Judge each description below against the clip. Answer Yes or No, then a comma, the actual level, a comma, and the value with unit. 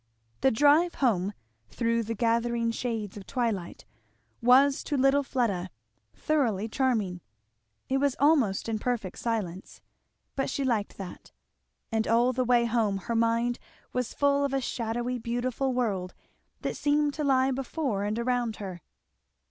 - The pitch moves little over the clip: No, average, 3.5 semitones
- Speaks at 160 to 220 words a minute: No, average, 145 wpm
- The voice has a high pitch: Yes, high, 235 Hz